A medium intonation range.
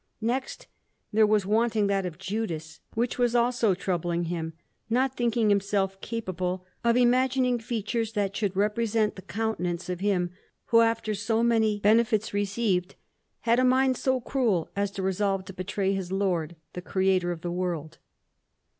Yes: average, 3.8 semitones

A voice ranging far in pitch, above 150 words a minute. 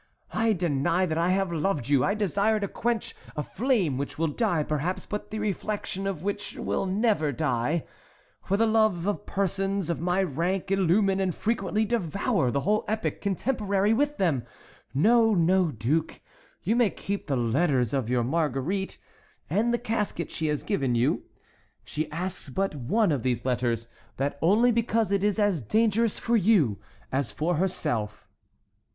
Yes: wide, 6.0 semitones; average, 170 wpm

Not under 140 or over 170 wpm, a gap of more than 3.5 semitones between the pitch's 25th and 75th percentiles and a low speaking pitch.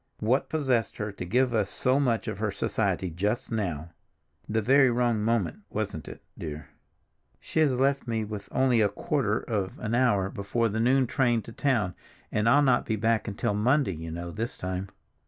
No: average, 180 wpm; average, 4.0 semitones; low, 110 Hz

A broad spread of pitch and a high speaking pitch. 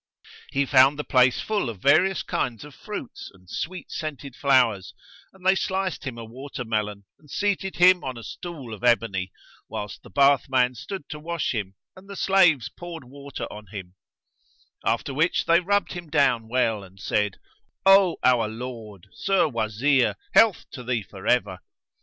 No: wide, 7.2 semitones; low, 130 Hz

